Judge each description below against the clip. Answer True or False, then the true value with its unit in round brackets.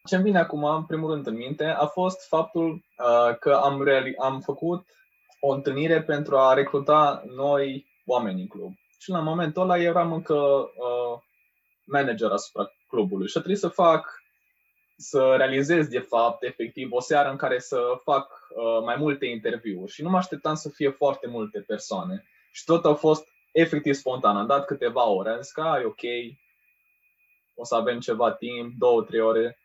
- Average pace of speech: False (175 wpm)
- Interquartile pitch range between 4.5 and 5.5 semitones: False (3.9 semitones)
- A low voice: False (145 Hz)